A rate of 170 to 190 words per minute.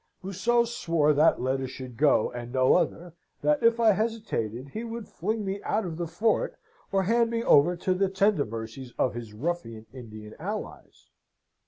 Yes: average, 175 wpm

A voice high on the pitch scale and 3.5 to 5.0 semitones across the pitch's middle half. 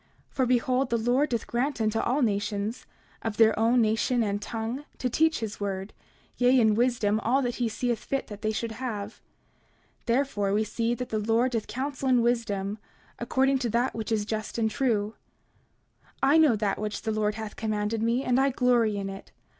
No: high, 230 Hz; average, 2.8 semitones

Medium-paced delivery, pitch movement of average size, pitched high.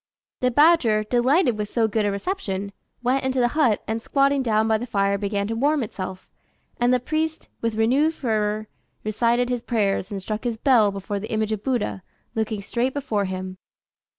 Yes: average, 185 wpm; average, 3.5 semitones; high, 225 Hz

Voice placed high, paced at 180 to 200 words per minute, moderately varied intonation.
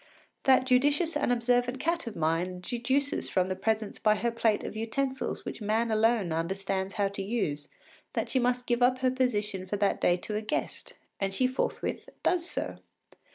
Yes: high, 225 Hz; average, 185 wpm; average, 4.5 semitones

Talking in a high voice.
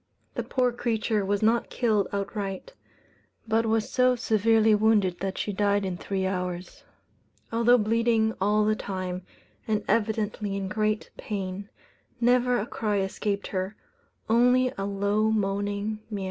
Yes: high, 210 Hz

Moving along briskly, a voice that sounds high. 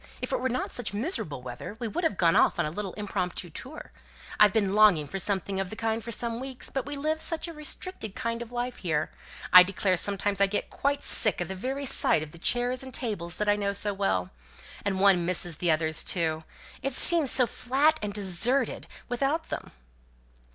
Yes: fast, 215 wpm; high, 210 Hz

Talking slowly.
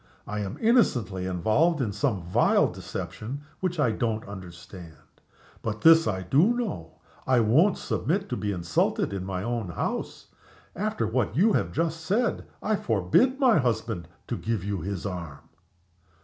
No: average, 155 wpm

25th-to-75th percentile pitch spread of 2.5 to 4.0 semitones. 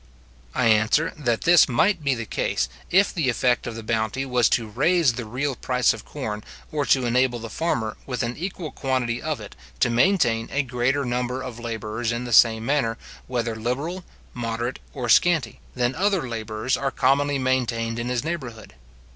Yes: average, 3.4 semitones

